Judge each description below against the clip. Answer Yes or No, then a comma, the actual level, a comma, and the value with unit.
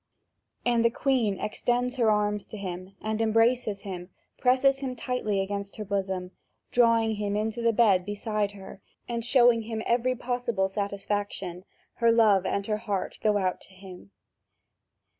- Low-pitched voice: No, high, 215 Hz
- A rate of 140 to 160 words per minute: Yes, average, 155 wpm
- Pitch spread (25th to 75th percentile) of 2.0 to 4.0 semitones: Yes, average, 2.9 semitones